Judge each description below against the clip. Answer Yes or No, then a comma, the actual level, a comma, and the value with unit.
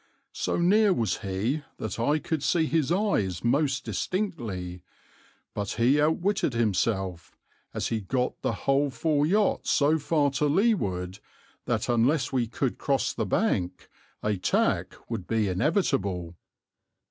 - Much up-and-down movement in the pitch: Yes, wide, 7.7 semitones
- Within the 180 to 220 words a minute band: No, slow, 135 wpm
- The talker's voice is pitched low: Yes, low, 130 Hz